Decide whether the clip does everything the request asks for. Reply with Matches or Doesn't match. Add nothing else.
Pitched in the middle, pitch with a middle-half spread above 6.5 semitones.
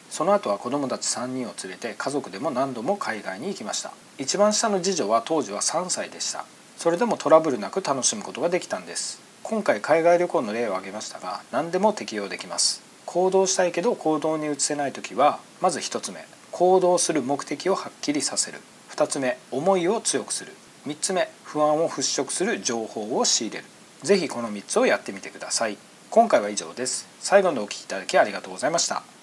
Matches